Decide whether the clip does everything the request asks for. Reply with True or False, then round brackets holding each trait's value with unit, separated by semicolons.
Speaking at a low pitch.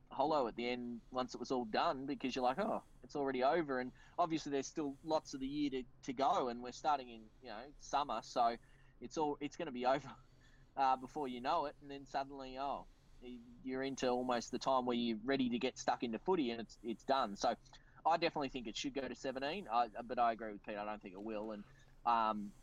True (130 Hz)